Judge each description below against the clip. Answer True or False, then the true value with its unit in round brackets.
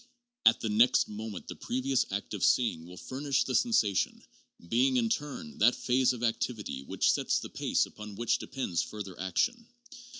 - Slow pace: False (170 wpm)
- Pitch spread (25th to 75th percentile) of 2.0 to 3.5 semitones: False (3.9 semitones)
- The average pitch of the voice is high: False (115 Hz)